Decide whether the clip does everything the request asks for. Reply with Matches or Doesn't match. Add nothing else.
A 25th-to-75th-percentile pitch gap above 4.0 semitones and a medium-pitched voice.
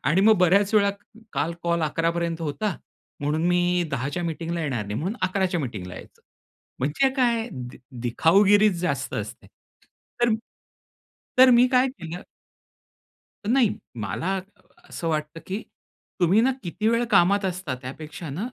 Matches